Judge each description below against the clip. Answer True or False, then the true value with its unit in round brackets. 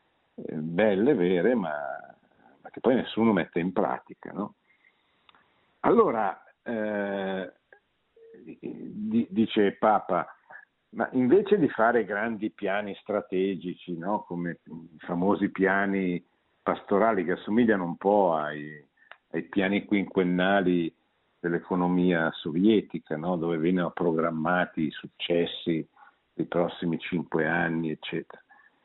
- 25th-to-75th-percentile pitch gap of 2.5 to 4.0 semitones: True (3.4 semitones)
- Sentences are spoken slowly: True (100 wpm)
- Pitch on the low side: True (90 Hz)